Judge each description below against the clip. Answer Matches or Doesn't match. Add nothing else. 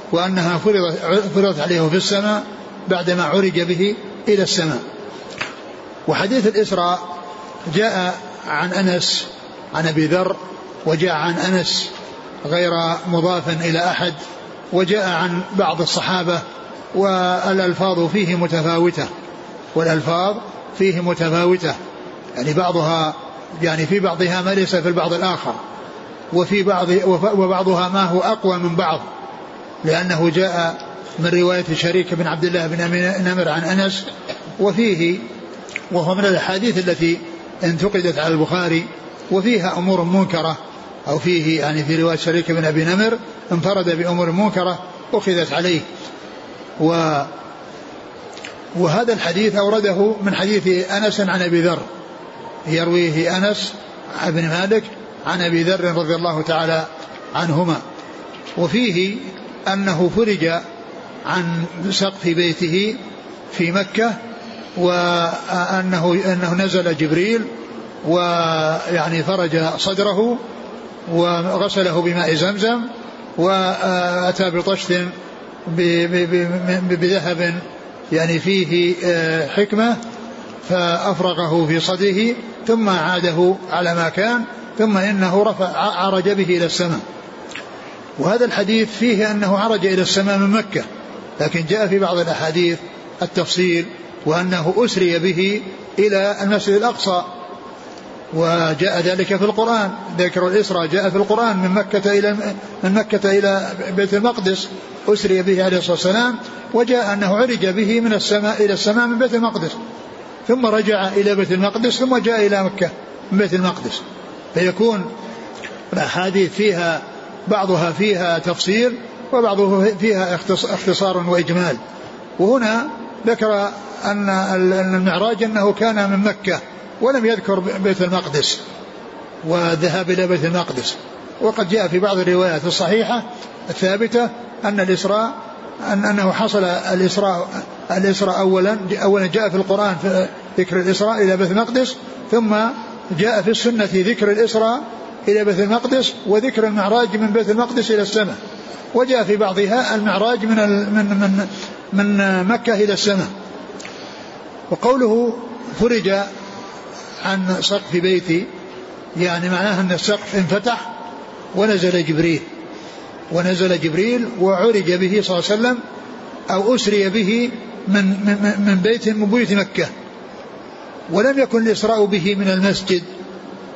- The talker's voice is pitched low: Doesn't match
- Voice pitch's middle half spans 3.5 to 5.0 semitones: Doesn't match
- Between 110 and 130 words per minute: Matches